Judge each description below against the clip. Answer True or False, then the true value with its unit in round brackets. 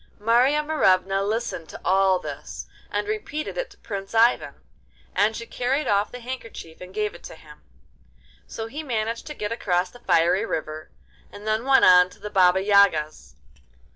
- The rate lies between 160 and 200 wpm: True (170 wpm)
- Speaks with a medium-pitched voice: False (210 Hz)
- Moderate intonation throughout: True (4.6 semitones)